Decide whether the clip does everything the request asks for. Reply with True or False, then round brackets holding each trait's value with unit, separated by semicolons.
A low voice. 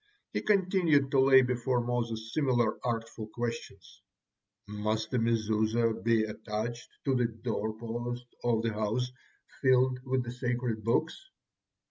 True (120 Hz)